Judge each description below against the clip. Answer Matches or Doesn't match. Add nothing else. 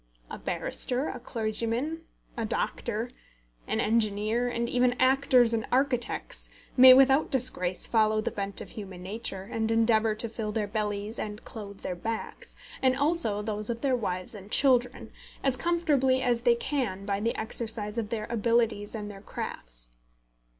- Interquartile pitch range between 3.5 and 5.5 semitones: Doesn't match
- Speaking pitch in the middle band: Doesn't match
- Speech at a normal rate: Matches